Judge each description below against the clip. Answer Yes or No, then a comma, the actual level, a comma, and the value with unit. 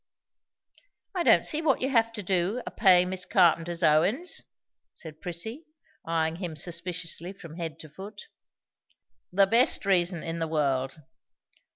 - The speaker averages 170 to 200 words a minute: No, average, 150 wpm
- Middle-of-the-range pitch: Yes, medium, 180 Hz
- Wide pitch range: No, average, 3.8 semitones